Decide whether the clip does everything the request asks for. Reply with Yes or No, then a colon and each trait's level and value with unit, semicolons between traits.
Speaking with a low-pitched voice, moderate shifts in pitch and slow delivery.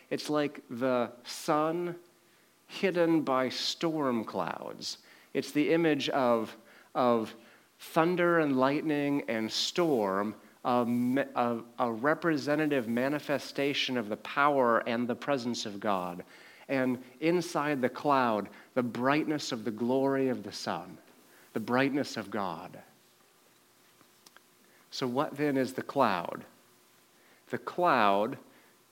Yes: low, 130 Hz; average, 4.3 semitones; slow, 115 wpm